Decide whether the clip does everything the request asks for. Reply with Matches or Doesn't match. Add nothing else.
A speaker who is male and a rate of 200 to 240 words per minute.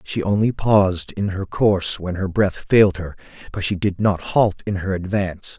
Matches